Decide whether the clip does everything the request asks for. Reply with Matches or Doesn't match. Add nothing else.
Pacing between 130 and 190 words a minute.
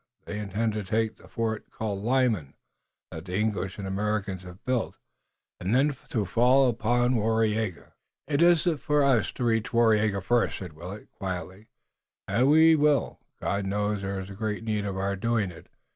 Matches